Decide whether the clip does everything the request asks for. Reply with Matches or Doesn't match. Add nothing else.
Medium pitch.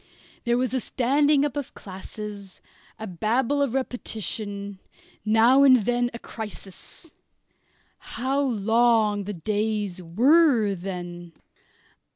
Doesn't match